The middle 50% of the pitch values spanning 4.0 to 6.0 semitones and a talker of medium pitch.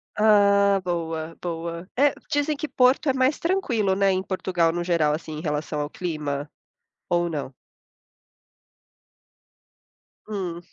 Yes: average, 4.5 semitones; medium, 175 Hz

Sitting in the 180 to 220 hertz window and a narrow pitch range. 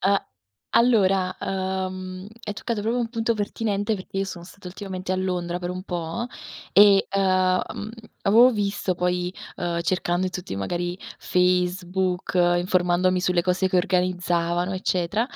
Yes: medium, 185 Hz; narrow, 1.8 semitones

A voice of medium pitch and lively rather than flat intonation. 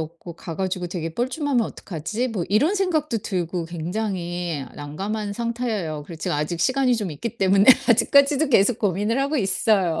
No: high, 200 Hz; wide, 5.8 semitones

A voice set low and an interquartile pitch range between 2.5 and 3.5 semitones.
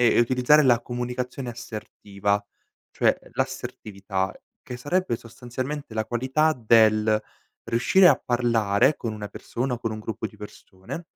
Yes: low, 120 Hz; average, 2.9 semitones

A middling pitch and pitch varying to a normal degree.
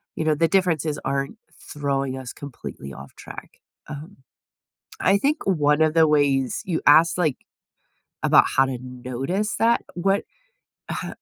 Yes: medium, 150 Hz; average, 4.4 semitones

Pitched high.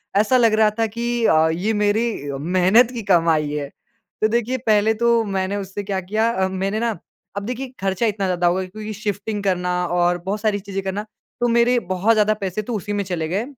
Yes: high, 205 Hz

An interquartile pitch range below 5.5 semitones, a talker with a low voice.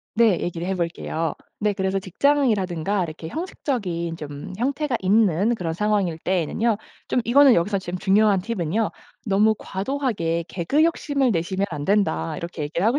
No: average, 5.1 semitones; high, 195 Hz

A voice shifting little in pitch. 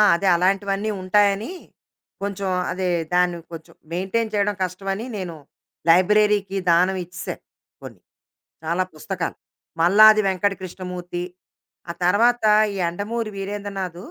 Yes: narrow, 2.3 semitones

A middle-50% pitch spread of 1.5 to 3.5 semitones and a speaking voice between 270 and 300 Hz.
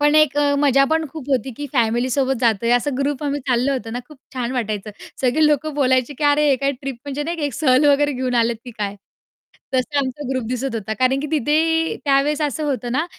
Yes: average, 2.8 semitones; very high, 275 Hz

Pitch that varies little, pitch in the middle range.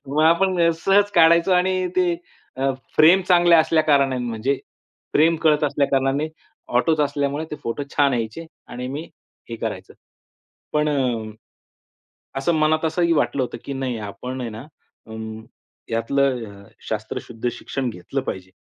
No: average, 4.4 semitones; medium, 145 Hz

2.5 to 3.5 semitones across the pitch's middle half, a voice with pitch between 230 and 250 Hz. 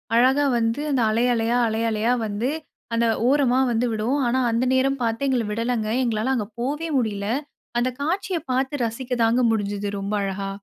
Yes: average, 3.0 semitones; high, 235 Hz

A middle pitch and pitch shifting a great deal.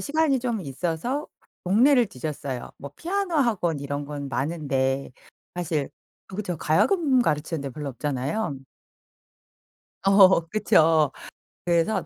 Yes: medium, 165 Hz; wide, 8.1 semitones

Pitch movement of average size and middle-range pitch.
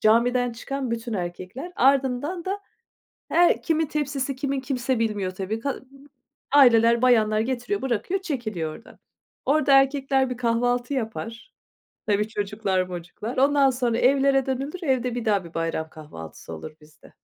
No: average, 4.2 semitones; high, 245 Hz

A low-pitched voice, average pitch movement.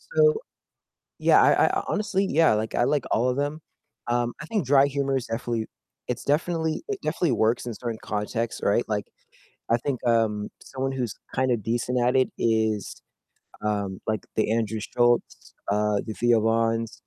Yes: low, 120 Hz; average, 3.6 semitones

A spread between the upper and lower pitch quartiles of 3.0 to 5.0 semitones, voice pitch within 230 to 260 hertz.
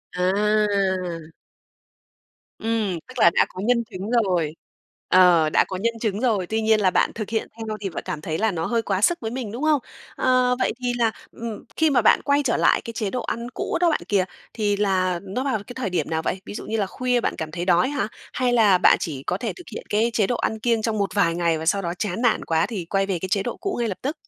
No: average, 4.3 semitones; high, 210 Hz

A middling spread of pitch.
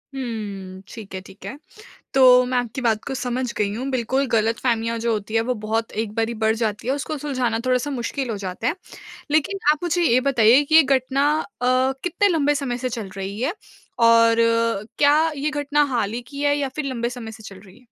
Yes: average, 3.6 semitones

